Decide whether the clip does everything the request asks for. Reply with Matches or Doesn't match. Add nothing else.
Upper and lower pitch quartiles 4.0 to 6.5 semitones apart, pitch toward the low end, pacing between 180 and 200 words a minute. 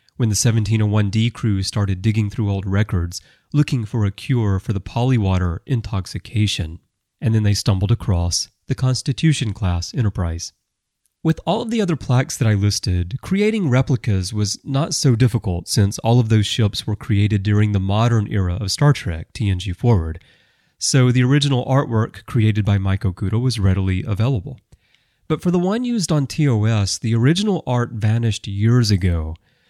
Doesn't match